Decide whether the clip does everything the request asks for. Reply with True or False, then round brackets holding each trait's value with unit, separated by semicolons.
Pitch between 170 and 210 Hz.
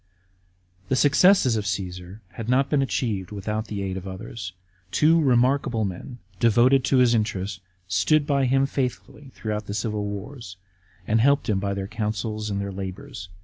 False (110 Hz)